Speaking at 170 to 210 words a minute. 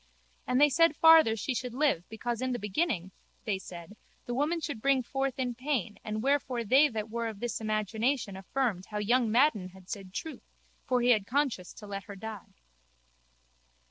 Yes: average, 185 wpm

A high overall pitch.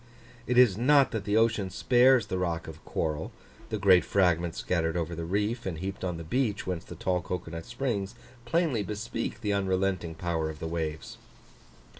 No: very low, 95 Hz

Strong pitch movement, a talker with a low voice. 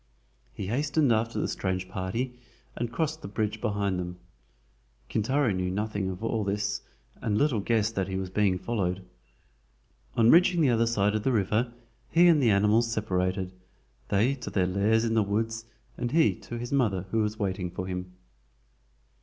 No: average, 3.6 semitones; low, 105 Hz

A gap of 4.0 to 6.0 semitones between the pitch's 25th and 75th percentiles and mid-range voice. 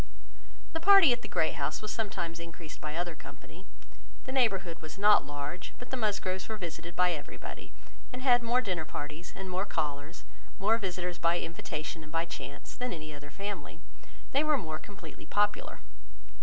Yes: average, 5.2 semitones; medium, 180 Hz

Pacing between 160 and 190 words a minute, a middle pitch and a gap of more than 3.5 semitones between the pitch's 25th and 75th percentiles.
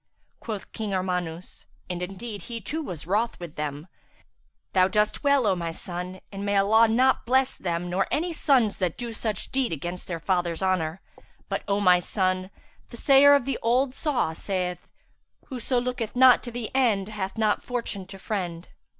No: average, 175 wpm; high, 200 Hz; average, 5.1 semitones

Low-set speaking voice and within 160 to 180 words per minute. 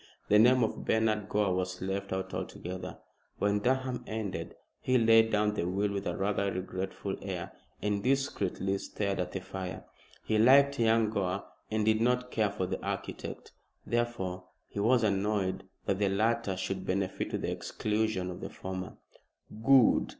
Yes: low, 105 Hz; average, 165 wpm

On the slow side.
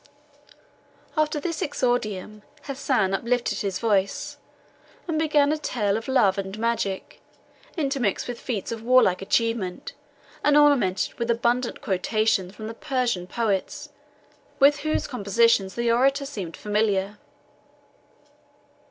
Yes: slow, 115 wpm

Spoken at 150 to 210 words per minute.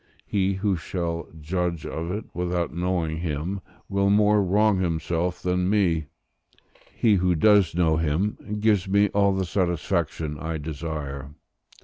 No: slow, 135 wpm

